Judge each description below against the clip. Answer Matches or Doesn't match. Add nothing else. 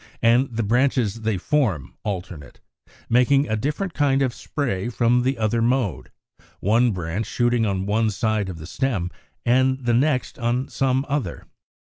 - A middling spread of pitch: Matches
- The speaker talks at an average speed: Matches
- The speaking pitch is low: Matches